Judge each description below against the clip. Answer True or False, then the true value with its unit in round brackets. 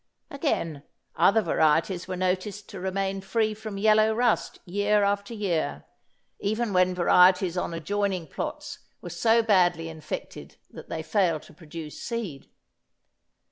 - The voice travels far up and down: False (3.7 semitones)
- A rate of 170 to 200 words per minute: False (135 wpm)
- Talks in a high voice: True (195 Hz)